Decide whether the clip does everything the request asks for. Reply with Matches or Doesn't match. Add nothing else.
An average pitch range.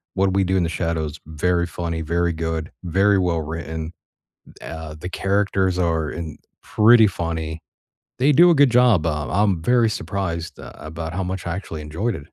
Matches